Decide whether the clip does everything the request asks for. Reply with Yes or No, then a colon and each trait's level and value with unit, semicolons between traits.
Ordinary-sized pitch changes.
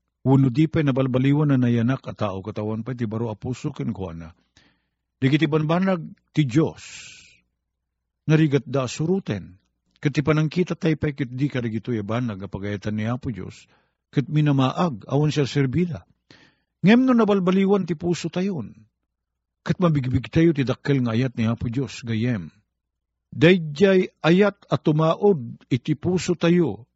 No: wide, 6.3 semitones